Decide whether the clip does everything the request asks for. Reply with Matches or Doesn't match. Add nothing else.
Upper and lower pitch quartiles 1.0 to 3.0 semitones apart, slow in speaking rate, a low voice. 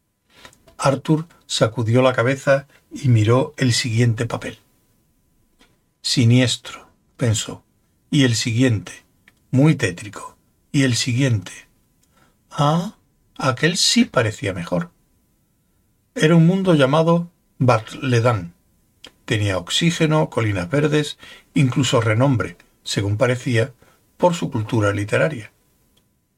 Doesn't match